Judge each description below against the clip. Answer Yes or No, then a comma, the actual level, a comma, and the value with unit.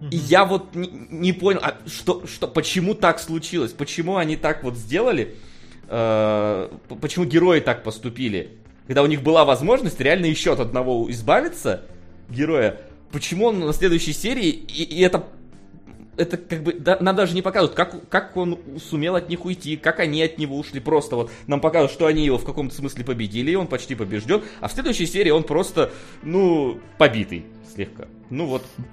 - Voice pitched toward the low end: No, medium, 155 Hz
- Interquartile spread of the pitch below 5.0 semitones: No, wide, 5.6 semitones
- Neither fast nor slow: No, fast, 175 wpm